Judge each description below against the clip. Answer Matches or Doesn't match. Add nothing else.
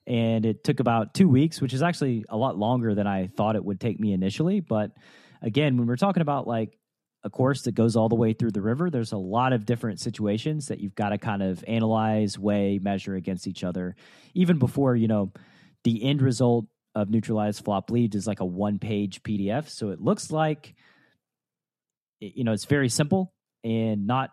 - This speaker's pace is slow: Doesn't match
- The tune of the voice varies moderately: Matches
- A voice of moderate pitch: Doesn't match